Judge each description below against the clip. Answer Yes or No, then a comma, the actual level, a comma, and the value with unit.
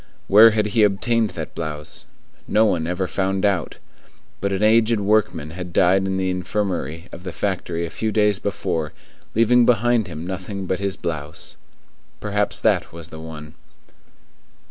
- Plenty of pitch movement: No, average, 3.8 semitones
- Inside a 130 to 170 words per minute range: Yes, average, 160 wpm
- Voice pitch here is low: Yes, very low, 95 Hz